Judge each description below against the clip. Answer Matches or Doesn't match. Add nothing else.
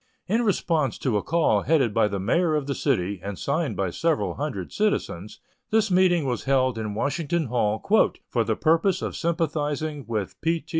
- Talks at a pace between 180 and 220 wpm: Matches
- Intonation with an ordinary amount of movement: Doesn't match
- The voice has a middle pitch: Matches